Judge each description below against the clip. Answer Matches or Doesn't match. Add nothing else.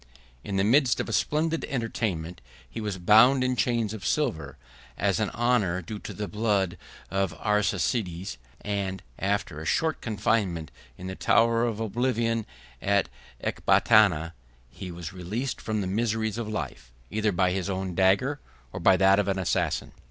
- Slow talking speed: Doesn't match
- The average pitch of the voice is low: Matches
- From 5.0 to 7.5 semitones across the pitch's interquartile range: Doesn't match